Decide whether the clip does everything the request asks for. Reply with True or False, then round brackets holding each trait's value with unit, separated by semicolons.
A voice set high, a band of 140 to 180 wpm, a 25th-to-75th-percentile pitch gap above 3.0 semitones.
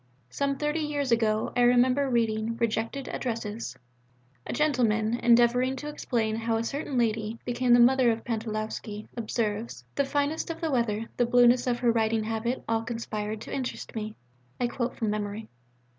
False (235 Hz; 170 wpm; 2.5 semitones)